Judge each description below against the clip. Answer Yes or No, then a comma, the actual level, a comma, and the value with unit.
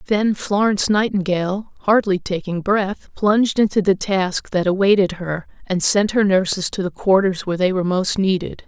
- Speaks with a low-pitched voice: No, high, 195 Hz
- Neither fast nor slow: Yes, average, 175 wpm